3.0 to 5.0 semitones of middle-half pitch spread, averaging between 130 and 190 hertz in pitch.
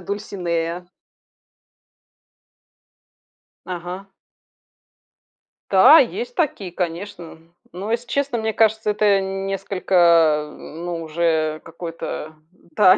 Yes: average, 3.6 semitones; medium, 185 Hz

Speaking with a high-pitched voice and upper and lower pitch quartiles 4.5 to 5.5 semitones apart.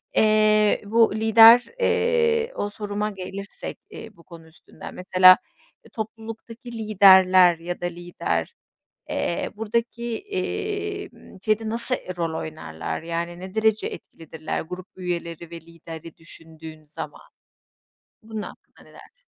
Yes: high, 205 Hz; average, 4.8 semitones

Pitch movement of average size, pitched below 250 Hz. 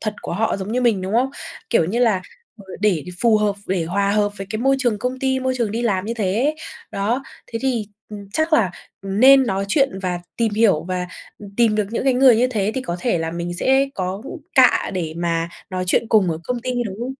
Yes: average, 4.7 semitones; high, 210 Hz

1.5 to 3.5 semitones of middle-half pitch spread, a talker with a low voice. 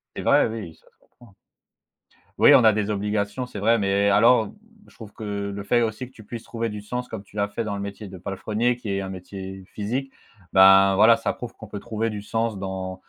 Yes: narrow, 2.5 semitones; low, 105 Hz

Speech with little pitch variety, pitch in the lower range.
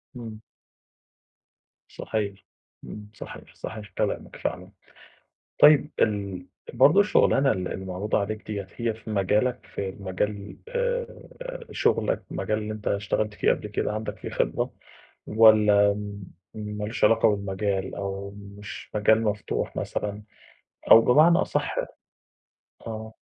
Yes: narrow, 1.9 semitones; low, 105 Hz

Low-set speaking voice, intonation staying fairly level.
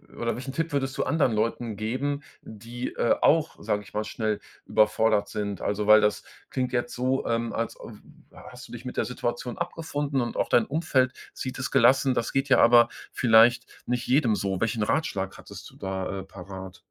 No: low, 120 Hz; average, 3.5 semitones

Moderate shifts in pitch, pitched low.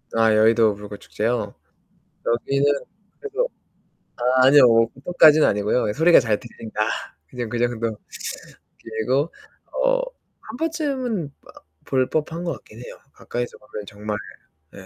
No: wide, 6.1 semitones; low, 120 Hz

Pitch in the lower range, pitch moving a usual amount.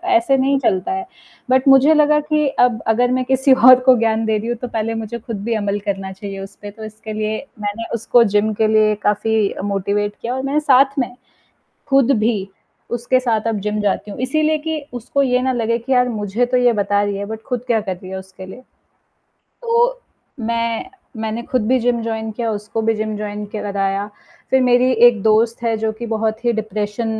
No: high, 225 Hz; average, 3.3 semitones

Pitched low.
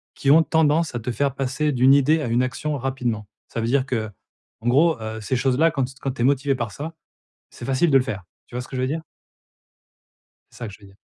Yes: low, 130 Hz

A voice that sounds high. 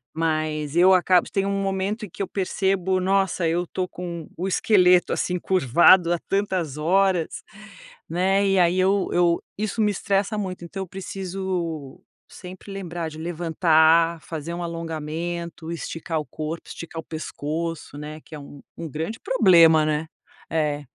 No: medium, 175 Hz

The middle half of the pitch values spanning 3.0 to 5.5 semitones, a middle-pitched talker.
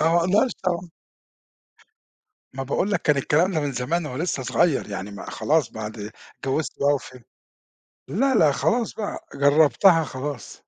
Yes: average, 4.7 semitones; medium, 150 Hz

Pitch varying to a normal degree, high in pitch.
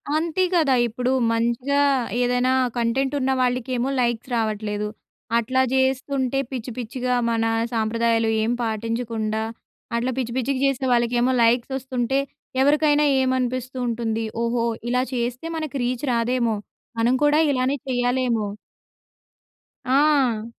No: narrow, 2.2 semitones; high, 245 Hz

